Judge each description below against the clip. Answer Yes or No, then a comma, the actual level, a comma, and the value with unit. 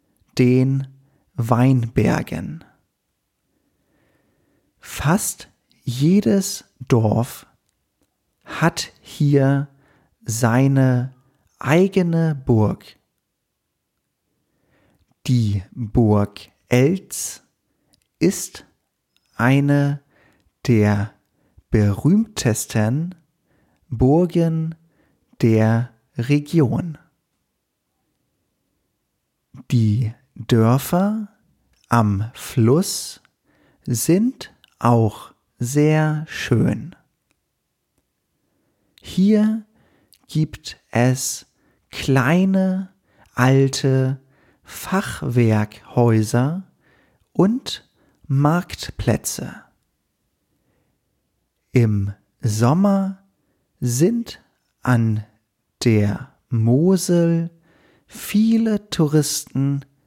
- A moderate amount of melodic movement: No, wide, 5.8 semitones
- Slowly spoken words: Yes, slow, 45 wpm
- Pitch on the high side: No, low, 135 Hz